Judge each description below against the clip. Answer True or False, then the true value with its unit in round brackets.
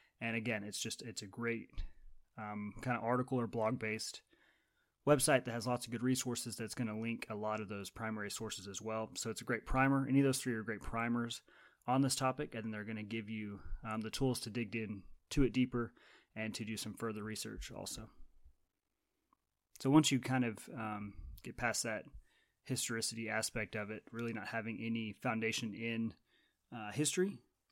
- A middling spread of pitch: False (2.2 semitones)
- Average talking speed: True (195 wpm)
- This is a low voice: True (115 Hz)